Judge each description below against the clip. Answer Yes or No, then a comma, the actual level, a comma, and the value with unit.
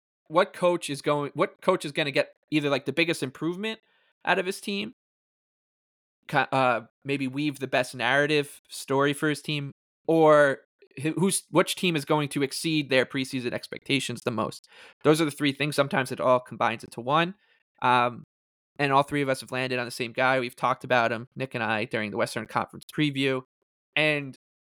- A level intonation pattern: No, average, 3.5 semitones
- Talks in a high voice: No, medium, 140 Hz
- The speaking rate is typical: Yes, average, 190 wpm